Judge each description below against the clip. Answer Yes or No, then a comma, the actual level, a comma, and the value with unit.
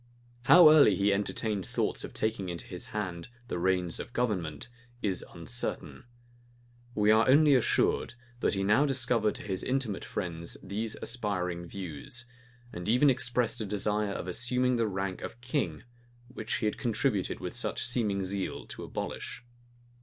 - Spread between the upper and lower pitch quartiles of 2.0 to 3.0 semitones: No, average, 4.5 semitones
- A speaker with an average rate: Yes, average, 155 wpm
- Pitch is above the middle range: No, low, 105 Hz